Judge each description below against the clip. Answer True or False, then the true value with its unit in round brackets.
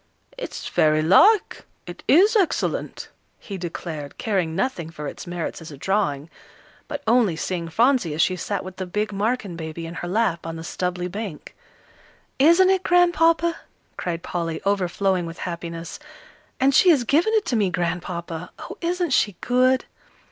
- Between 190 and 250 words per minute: False (160 wpm)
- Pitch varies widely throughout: True (7.4 semitones)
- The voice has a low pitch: False (185 Hz)